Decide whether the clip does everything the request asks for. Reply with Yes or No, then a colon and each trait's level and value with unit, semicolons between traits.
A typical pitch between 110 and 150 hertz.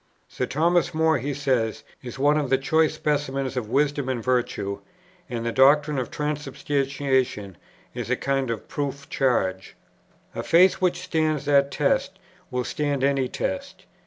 Yes: medium, 140 Hz